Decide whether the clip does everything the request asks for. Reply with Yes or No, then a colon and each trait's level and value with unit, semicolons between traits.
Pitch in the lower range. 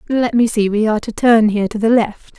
No: high, 220 Hz